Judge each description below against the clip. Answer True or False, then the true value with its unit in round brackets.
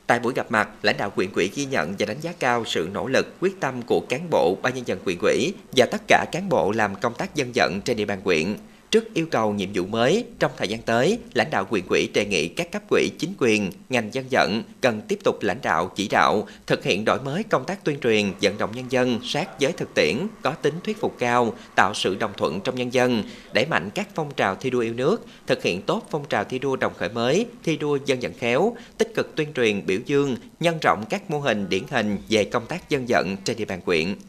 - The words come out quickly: True (255 wpm)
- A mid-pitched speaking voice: False (130 Hz)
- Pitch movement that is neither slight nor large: False (6.1 semitones)